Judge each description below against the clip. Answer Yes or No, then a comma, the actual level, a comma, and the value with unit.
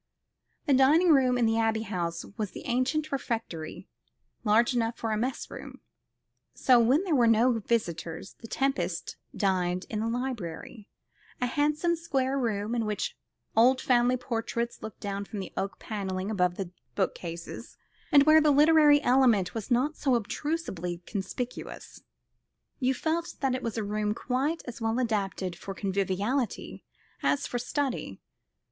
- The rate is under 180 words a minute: Yes, average, 150 wpm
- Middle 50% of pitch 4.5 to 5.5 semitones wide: Yes, average, 4.8 semitones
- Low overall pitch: No, high, 235 Hz